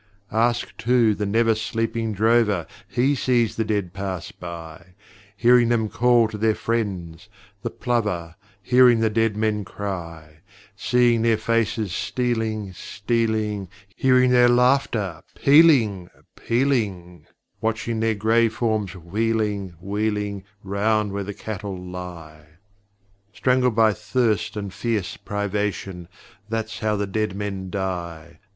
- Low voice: Yes, low, 110 Hz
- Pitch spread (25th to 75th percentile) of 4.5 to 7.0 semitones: No, average, 3.2 semitones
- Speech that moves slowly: Yes, slow, 120 wpm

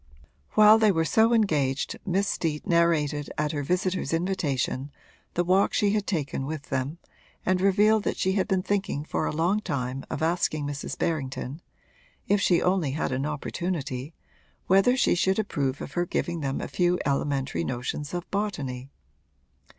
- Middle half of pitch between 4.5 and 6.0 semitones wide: Yes, average, 5.2 semitones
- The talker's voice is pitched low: No, medium, 165 Hz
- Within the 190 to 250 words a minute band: No, average, 165 wpm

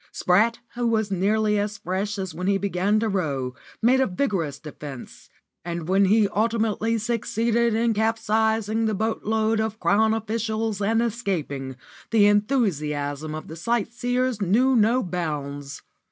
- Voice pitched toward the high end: Yes, high, 210 Hz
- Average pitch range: Yes, average, 3.8 semitones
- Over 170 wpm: No, average, 140 wpm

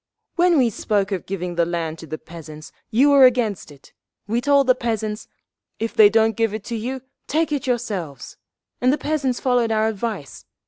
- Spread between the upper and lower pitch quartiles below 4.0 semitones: No, average, 4.8 semitones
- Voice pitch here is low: No, high, 225 Hz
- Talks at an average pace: Yes, average, 190 wpm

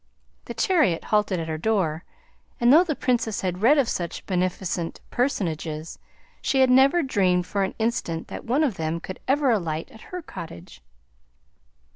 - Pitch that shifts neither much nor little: No, wide, 7.6 semitones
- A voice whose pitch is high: Yes, high, 200 Hz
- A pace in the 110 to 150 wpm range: No, average, 160 wpm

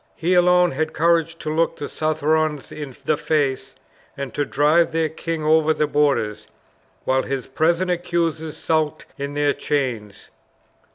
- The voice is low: No, medium, 155 Hz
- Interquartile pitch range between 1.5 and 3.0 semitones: Yes, narrow, 2.4 semitones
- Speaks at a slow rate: No, average, 150 wpm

